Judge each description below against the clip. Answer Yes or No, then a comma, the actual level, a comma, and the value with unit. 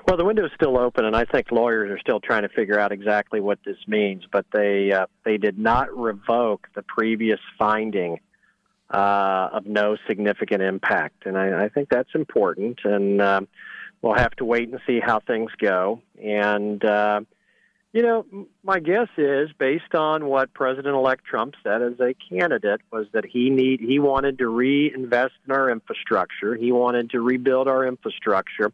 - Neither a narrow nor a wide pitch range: Yes, average, 4.2 semitones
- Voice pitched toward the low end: Yes, low, 120 Hz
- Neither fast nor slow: Yes, average, 180 wpm